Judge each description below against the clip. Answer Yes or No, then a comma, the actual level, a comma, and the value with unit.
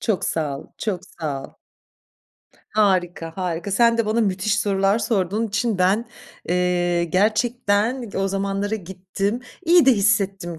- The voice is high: Yes, high, 195 Hz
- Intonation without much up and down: No, average, 3.3 semitones